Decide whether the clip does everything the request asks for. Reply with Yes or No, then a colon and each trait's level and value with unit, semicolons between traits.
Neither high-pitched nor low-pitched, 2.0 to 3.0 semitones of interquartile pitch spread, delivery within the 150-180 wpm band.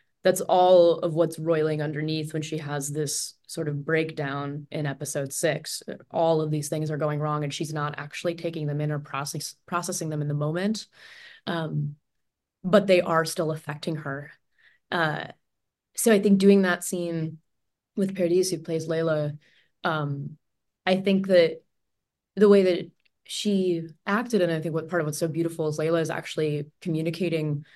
Yes: medium, 160 Hz; average, 2.7 semitones; average, 170 wpm